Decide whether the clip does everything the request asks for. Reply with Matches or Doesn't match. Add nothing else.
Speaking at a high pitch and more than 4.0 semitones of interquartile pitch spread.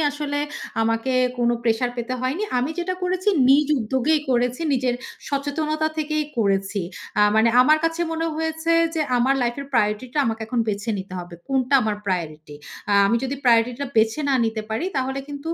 Matches